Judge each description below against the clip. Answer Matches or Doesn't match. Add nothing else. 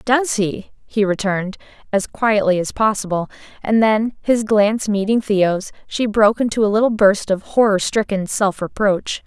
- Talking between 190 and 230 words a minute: Doesn't match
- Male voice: Doesn't match